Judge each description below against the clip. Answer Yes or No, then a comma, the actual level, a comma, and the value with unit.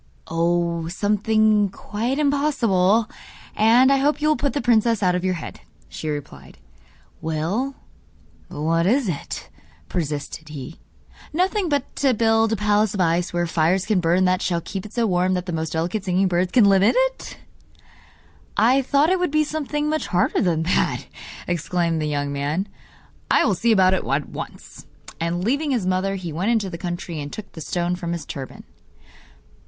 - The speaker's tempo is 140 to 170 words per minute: No, average, 180 wpm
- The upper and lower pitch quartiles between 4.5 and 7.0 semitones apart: Yes, wide, 5.5 semitones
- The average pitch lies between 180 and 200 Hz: Yes, medium, 185 Hz